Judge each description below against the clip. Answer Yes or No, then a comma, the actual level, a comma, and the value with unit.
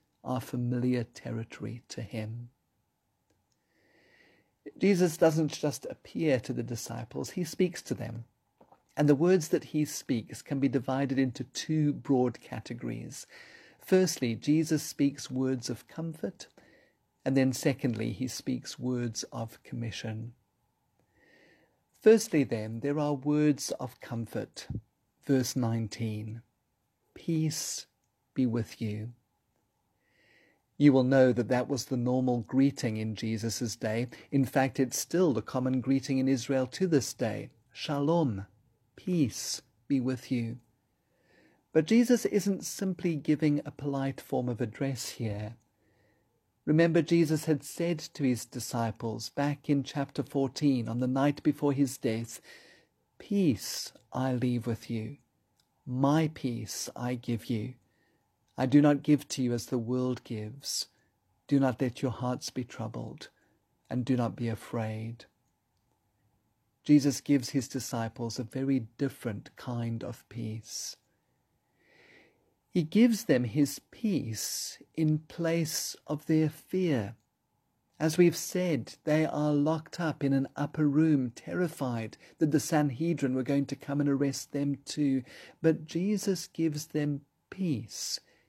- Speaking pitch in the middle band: No, low, 130 Hz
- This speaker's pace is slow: Yes, slow, 130 wpm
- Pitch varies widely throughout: No, average, 4.1 semitones